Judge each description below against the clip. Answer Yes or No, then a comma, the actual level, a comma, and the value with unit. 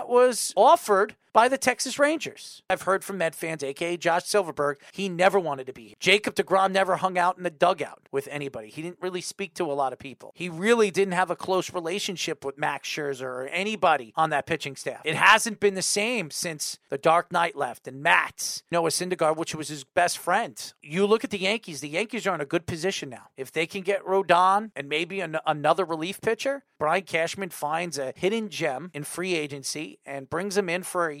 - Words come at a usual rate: No, fast, 215 wpm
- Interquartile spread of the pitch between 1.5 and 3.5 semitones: No, average, 4.1 semitones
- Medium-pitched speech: Yes, medium, 175 Hz